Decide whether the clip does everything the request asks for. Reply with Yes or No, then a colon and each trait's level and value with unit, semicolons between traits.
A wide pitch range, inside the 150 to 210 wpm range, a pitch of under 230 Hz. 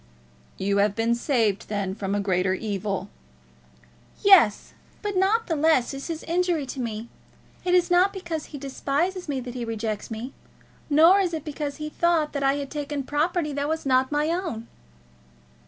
No: wide, 6.7 semitones; average, 175 wpm; very high, 285 Hz